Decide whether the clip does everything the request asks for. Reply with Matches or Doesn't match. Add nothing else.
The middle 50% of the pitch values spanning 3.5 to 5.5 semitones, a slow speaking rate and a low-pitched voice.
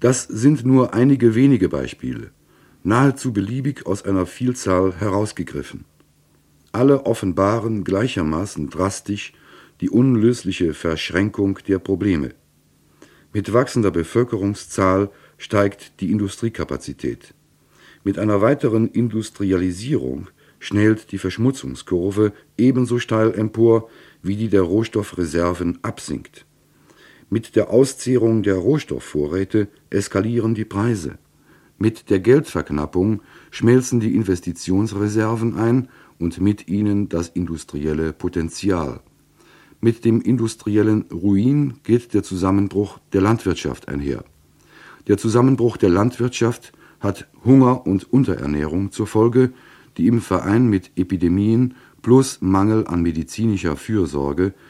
Matches